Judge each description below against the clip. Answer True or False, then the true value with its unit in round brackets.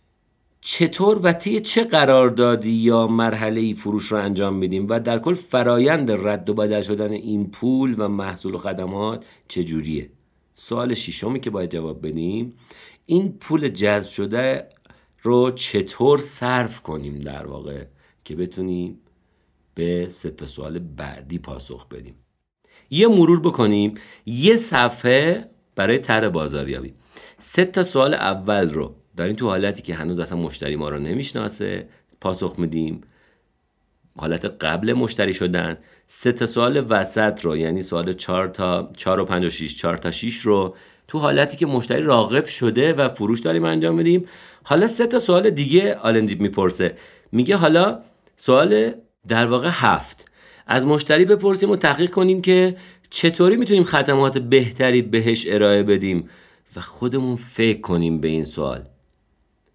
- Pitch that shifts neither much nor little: False (6.9 semitones)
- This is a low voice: True (105 Hz)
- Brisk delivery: False (145 wpm)